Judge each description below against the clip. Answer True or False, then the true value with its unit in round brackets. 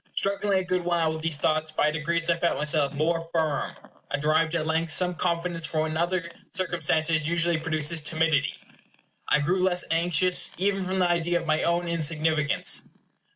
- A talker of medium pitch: True (165 Hz)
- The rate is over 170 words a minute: True (180 wpm)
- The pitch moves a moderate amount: False (1.8 semitones)